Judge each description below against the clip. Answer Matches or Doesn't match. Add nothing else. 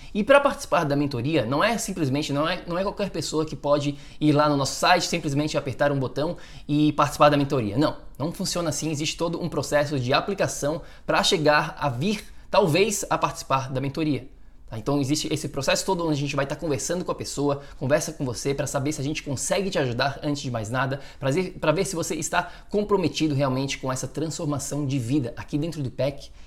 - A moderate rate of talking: Doesn't match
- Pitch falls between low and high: Matches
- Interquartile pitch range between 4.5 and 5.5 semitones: Doesn't match